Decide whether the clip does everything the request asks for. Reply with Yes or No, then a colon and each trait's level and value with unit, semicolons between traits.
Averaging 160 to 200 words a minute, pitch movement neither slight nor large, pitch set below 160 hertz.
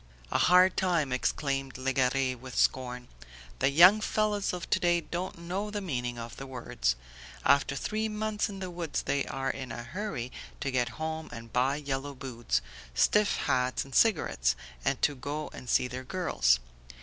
No: average, 175 wpm; wide, 6.1 semitones; medium, 140 Hz